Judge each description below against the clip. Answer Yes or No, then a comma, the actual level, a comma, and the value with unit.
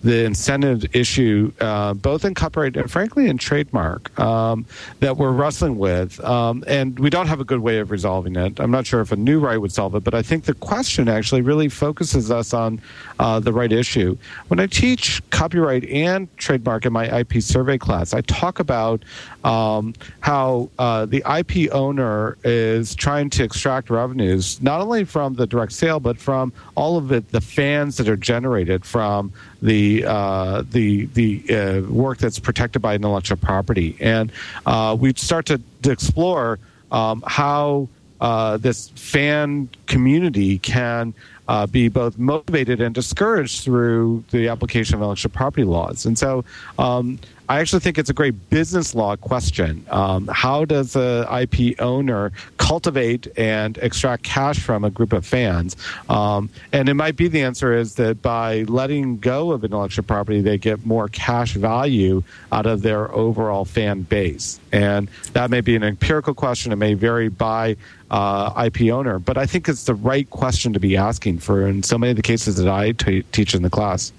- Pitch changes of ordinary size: Yes, average, 4.0 semitones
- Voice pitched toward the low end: Yes, low, 115 Hz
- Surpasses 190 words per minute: No, average, 180 wpm